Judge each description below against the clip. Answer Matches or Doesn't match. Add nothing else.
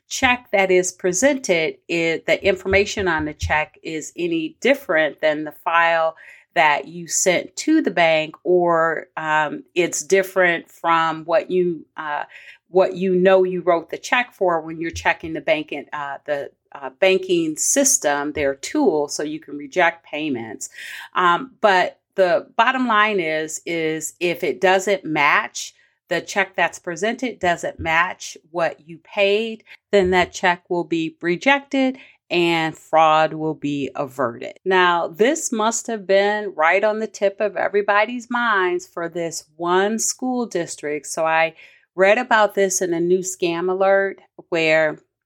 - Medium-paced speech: Matches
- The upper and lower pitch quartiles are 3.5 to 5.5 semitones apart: Matches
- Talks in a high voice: Doesn't match